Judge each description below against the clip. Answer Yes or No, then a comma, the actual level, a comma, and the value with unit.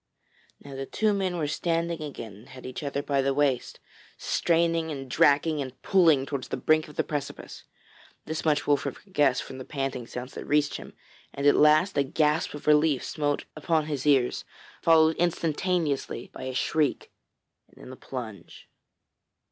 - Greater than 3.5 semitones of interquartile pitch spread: No, average, 3.0 semitones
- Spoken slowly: No, average, 175 wpm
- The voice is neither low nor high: Yes, medium, 145 Hz